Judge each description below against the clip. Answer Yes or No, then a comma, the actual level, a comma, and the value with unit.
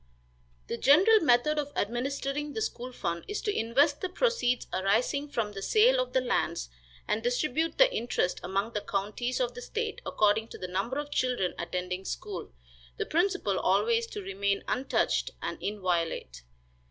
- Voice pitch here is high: Yes, high, 240 Hz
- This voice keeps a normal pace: Yes, average, 165 wpm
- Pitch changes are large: Yes, wide, 6.9 semitones